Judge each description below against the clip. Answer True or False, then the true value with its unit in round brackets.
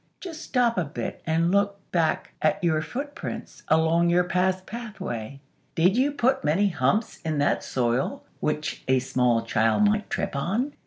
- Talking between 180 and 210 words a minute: False (160 wpm)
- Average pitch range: False (6.2 semitones)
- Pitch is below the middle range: False (175 Hz)